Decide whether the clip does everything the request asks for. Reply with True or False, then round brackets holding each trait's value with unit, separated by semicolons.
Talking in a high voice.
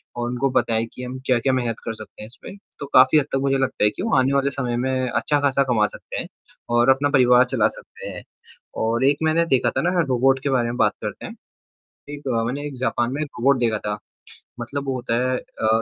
False (130 Hz)